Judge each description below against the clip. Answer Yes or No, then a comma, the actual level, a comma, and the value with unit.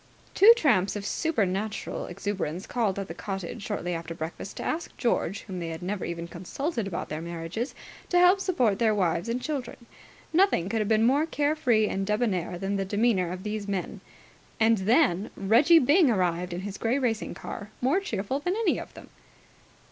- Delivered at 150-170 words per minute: No, average, 185 wpm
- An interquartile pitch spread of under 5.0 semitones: No, average, 5.3 semitones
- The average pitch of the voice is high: Yes, high, 210 Hz